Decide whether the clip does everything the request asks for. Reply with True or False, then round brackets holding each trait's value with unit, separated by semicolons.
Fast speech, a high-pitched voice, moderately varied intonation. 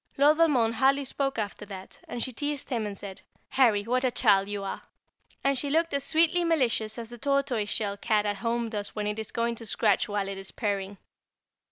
True (215 wpm; 230 Hz; 4.9 semitones)